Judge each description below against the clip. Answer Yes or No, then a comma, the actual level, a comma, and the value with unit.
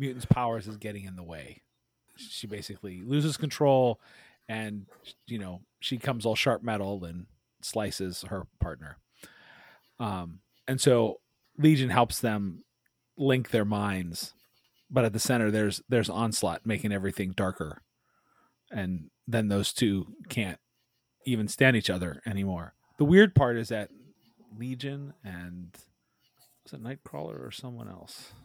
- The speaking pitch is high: No, low, 110 Hz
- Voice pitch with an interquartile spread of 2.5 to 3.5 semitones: No, average, 4.7 semitones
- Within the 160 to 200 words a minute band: No, slow, 135 wpm